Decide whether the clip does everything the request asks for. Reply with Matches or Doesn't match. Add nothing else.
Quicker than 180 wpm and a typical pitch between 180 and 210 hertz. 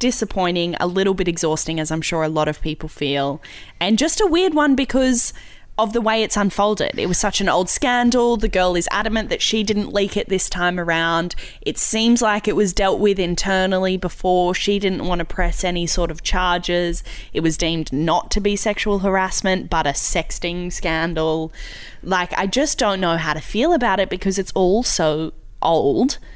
Matches